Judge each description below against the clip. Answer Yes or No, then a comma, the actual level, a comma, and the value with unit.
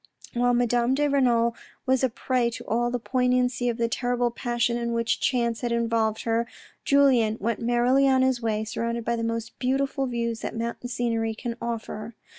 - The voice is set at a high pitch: Yes, high, 235 Hz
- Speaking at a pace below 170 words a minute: No, average, 185 wpm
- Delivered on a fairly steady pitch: Yes, narrow, 1.4 semitones